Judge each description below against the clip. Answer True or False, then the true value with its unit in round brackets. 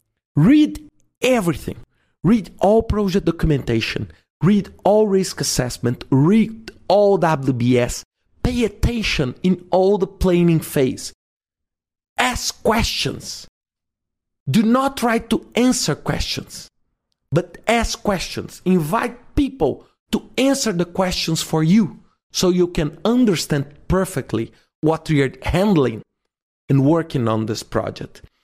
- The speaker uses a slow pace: True (110 wpm)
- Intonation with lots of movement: True (7.7 semitones)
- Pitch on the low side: False (170 Hz)